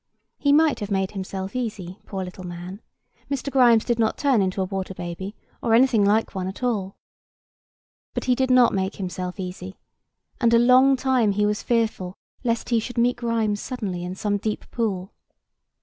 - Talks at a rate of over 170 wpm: Yes, average, 180 wpm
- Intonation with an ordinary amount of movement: Yes, average, 4.2 semitones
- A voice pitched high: Yes, high, 210 Hz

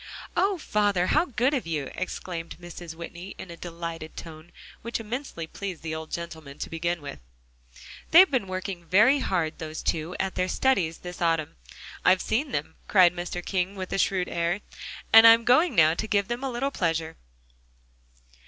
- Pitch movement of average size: Yes, average, 4.7 semitones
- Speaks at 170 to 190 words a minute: Yes, average, 175 wpm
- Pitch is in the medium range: Yes, medium, 180 Hz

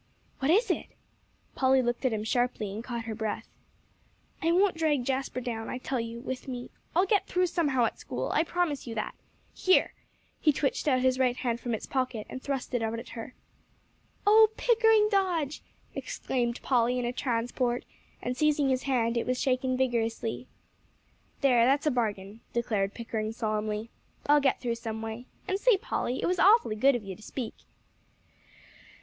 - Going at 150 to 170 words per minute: No, average, 180 wpm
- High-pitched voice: Yes, very high, 250 Hz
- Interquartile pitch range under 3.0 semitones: No, average, 4.0 semitones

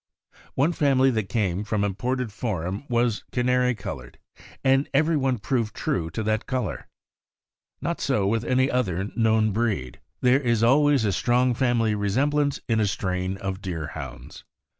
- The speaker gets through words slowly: No, average, 150 wpm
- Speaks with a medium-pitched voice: No, low, 115 Hz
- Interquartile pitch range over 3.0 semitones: Yes, average, 4.4 semitones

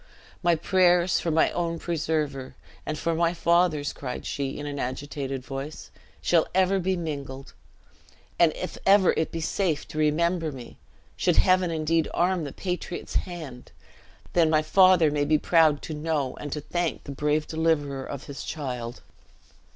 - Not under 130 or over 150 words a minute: No, average, 160 wpm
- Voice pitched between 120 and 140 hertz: No, medium, 155 Hz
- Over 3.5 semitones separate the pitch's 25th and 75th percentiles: No, average, 3.2 semitones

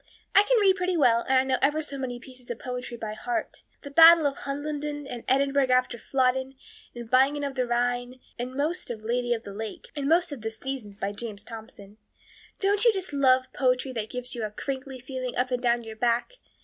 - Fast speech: Yes, fast, 225 wpm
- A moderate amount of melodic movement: Yes, average, 3.0 semitones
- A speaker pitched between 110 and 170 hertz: No, very high, 255 Hz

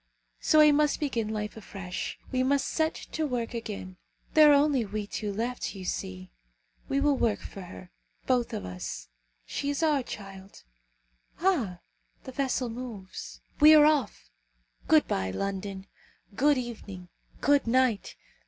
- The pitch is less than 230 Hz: No, high, 235 Hz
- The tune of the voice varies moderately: No, wide, 6.3 semitones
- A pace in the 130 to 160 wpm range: Yes, average, 150 wpm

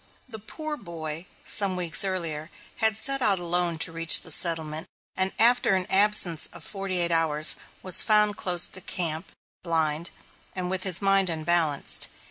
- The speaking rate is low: No, average, 160 wpm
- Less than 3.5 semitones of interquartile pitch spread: Yes, average, 3.1 semitones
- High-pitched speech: No, medium, 180 Hz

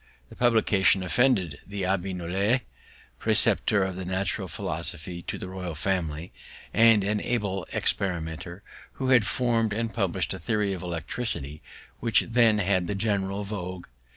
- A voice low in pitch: Yes, very low, 95 Hz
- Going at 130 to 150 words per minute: Yes, average, 140 wpm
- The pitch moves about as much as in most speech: Yes, average, 3.3 semitones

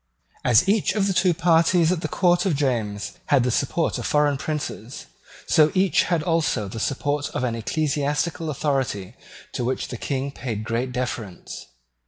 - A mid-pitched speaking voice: Yes, medium, 145 Hz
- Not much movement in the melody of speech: No, average, 5.0 semitones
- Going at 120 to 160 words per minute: No, average, 170 wpm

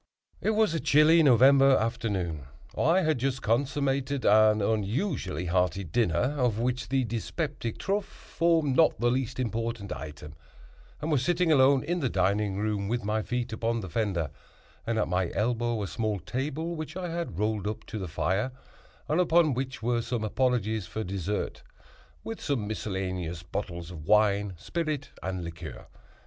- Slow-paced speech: No, average, 160 wpm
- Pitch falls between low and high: No, low, 115 Hz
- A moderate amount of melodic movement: No, wide, 5.7 semitones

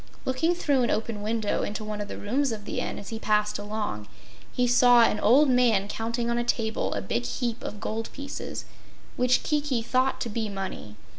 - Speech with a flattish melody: No, average, 3.1 semitones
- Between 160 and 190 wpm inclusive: No, fast, 205 wpm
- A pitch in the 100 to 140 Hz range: No, high, 225 Hz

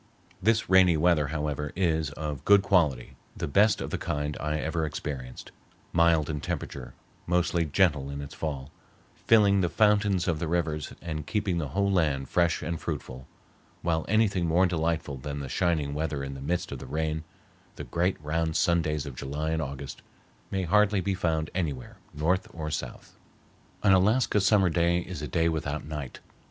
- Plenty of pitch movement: No, average, 3.6 semitones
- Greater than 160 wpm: Yes, average, 175 wpm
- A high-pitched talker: No, very low, 80 Hz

